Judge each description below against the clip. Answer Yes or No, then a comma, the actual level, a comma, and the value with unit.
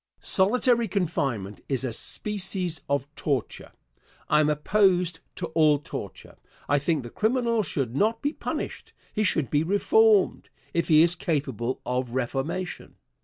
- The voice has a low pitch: No, medium, 160 Hz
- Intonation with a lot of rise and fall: Yes, wide, 6.7 semitones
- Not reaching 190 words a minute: Yes, average, 145 wpm